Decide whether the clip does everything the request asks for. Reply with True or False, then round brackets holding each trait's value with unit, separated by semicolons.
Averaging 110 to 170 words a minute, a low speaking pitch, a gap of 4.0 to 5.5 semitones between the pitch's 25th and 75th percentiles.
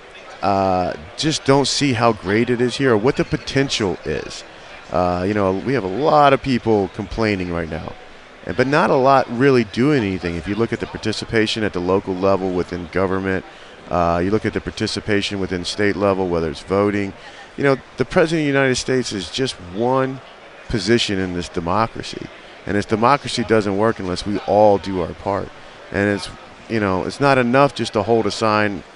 False (195 wpm; 105 Hz; 4.5 semitones)